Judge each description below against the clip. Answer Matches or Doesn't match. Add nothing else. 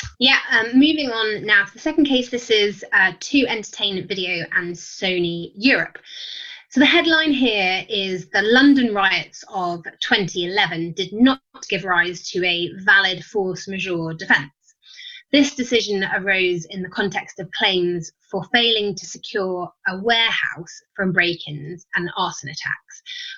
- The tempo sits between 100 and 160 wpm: Matches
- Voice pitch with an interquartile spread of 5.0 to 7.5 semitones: Matches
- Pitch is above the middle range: Matches